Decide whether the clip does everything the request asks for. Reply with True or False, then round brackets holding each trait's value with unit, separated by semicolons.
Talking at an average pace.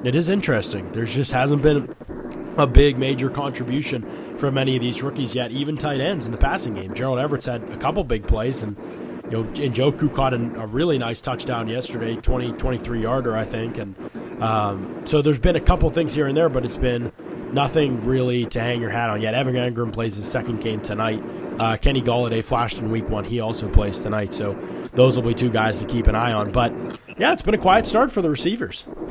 False (220 wpm)